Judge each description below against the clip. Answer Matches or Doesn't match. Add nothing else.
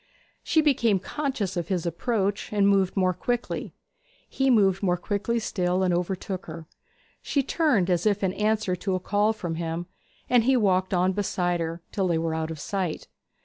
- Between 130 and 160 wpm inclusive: Doesn't match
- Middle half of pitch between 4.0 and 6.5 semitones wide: Doesn't match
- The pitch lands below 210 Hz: Matches